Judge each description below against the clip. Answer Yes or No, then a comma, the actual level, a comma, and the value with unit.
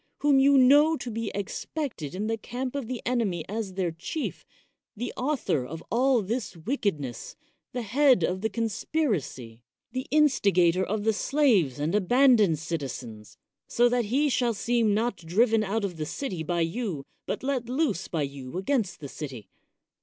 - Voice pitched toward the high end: Yes, high, 215 Hz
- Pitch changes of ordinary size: No, wide, 7.1 semitones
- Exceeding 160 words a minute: Yes, average, 170 wpm